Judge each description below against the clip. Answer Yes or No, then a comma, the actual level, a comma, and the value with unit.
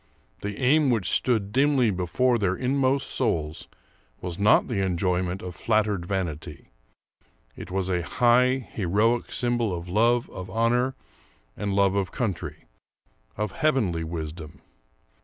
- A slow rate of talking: Yes, slow, 130 wpm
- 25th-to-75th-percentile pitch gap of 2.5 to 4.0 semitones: No, average, 5.1 semitones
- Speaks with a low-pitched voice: Yes, low, 100 Hz